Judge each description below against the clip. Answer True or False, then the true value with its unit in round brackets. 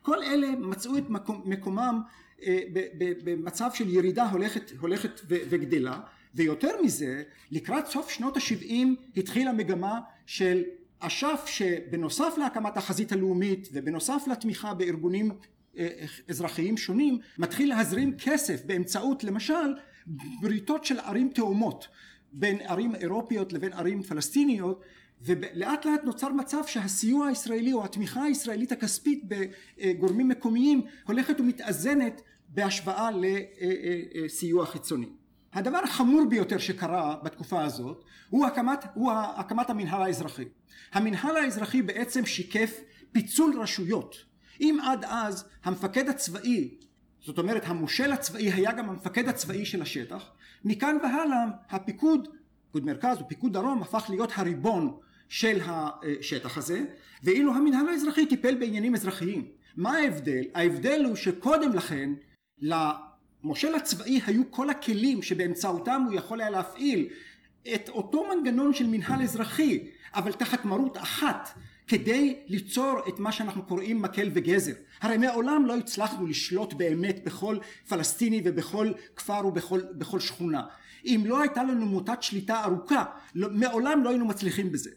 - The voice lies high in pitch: True (220 Hz)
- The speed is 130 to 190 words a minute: False (120 wpm)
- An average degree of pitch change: False (6.1 semitones)